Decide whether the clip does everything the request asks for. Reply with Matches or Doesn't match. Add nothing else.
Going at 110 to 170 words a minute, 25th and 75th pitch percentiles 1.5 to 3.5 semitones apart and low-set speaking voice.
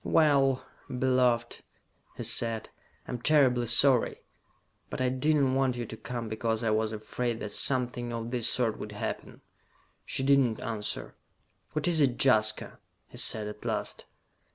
Matches